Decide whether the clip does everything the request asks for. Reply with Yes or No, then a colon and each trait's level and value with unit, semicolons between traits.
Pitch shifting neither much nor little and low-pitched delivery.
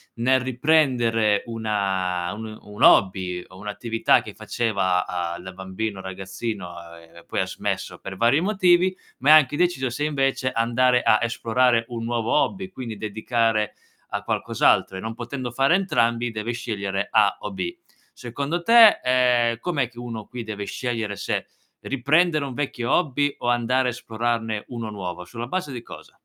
Yes: average, 4.0 semitones; low, 115 Hz